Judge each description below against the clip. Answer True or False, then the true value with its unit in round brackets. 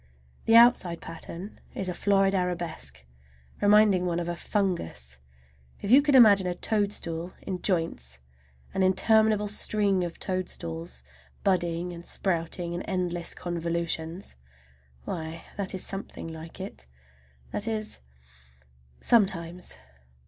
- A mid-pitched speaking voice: True (180 Hz)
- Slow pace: True (115 wpm)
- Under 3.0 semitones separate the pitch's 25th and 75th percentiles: False (3.3 semitones)